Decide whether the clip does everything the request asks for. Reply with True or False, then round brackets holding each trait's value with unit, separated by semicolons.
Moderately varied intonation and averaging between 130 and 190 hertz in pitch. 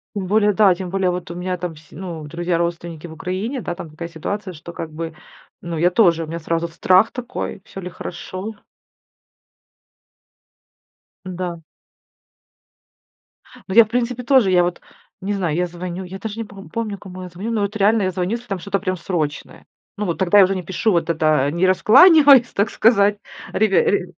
True (3.2 semitones; 185 Hz)